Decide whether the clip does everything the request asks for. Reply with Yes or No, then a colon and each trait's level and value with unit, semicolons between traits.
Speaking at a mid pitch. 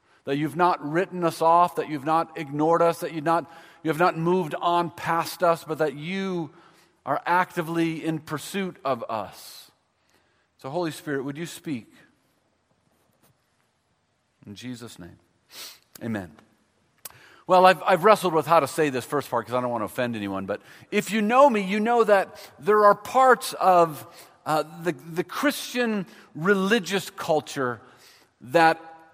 Yes: medium, 165 Hz